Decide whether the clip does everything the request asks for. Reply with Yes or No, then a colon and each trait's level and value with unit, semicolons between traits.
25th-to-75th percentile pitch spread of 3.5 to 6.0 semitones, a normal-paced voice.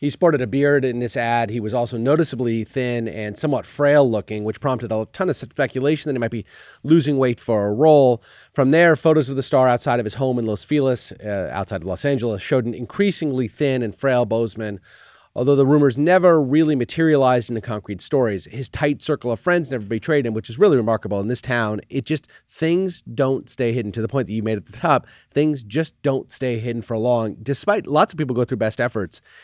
No: average, 4.3 semitones; fast, 220 wpm